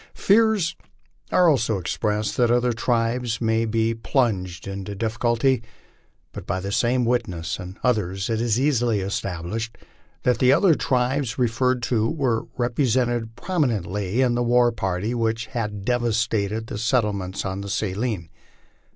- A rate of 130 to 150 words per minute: Yes, average, 140 wpm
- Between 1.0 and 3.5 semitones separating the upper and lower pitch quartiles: Yes, average, 3.2 semitones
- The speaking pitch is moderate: No, low, 115 Hz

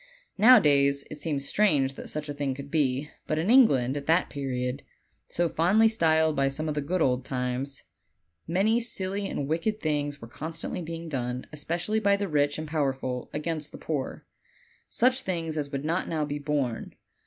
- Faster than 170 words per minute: Yes, average, 180 wpm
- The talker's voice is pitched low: No, medium, 150 Hz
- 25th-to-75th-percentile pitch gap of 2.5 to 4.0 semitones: Yes, average, 3.4 semitones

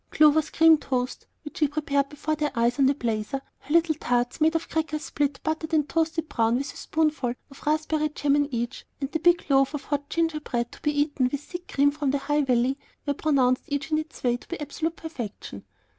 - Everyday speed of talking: No, fast, 220 wpm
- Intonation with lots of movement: No, narrow, 2.6 semitones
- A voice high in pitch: Yes, very high, 290 Hz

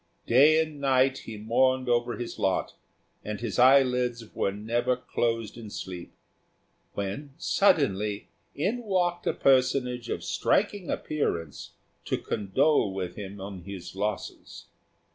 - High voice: No, low, 120 Hz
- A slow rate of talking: Yes, slow, 125 wpm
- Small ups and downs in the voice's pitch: No, average, 5.1 semitones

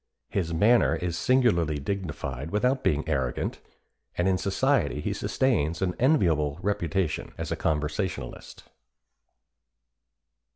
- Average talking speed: No, slow, 110 wpm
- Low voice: Yes, very low, 85 Hz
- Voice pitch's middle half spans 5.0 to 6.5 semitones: Yes, wide, 5.5 semitones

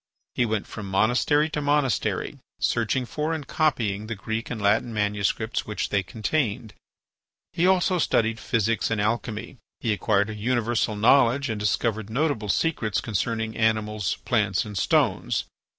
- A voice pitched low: Yes, low, 110 Hz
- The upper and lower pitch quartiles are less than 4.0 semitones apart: Yes, average, 3.1 semitones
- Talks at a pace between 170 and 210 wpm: No, average, 145 wpm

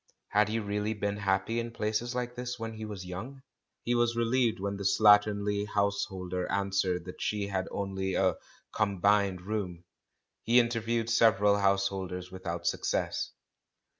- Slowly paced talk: No, average, 150 wpm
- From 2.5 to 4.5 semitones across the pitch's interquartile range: Yes, average, 2.9 semitones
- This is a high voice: No, low, 100 Hz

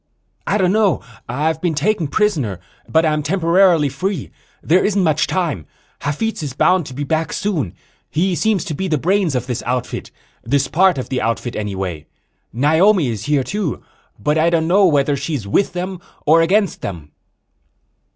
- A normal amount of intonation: No, wide, 5.9 semitones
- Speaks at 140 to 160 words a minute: No, average, 170 wpm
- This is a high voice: No, medium, 160 Hz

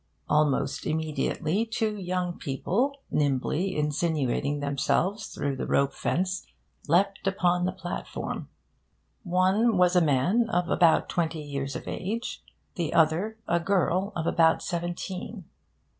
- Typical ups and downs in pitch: Yes, average, 4.0 semitones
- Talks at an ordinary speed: No, slow, 125 wpm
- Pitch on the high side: No, medium, 175 Hz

